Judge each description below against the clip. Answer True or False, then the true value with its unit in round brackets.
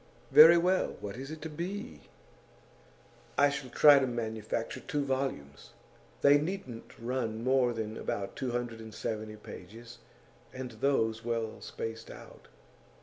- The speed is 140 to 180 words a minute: True (145 wpm)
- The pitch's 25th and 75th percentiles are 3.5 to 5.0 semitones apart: True (3.8 semitones)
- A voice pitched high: False (120 Hz)